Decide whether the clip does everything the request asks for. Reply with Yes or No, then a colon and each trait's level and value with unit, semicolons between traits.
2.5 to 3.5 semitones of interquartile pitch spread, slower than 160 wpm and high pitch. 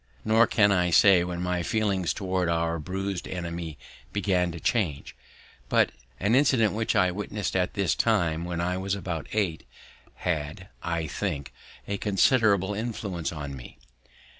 No: average, 3.2 semitones; average, 150 wpm; very low, 90 Hz